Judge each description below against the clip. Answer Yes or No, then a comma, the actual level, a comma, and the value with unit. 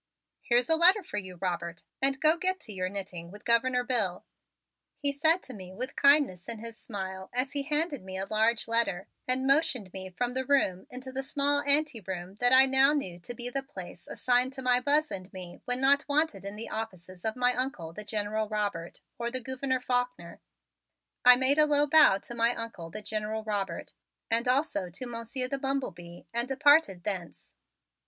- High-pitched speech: Yes, high, 240 Hz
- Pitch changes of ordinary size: No, wide, 5.7 semitones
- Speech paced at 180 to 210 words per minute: Yes, average, 195 wpm